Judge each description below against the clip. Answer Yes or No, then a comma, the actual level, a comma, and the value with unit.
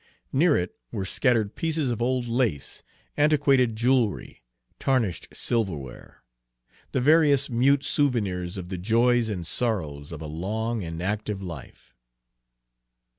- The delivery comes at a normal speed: No, slow, 125 wpm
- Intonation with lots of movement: Yes, wide, 6.0 semitones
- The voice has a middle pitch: No, low, 115 Hz